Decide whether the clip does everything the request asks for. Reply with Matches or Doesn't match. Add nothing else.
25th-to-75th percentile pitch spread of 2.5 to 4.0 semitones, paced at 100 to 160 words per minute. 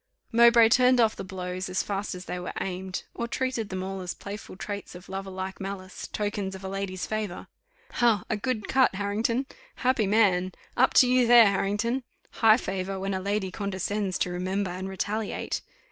Doesn't match